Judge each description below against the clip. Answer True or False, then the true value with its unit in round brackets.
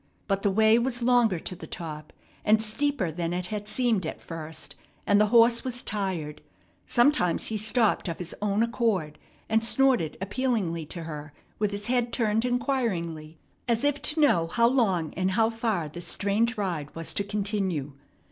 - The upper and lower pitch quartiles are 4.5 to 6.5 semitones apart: True (5.6 semitones)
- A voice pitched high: True (210 Hz)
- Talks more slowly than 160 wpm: False (175 wpm)